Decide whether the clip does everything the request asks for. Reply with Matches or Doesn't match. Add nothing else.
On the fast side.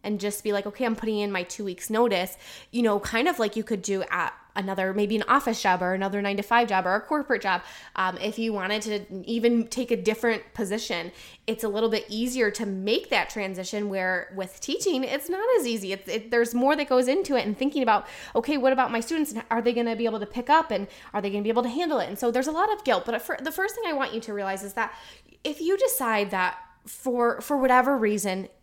Matches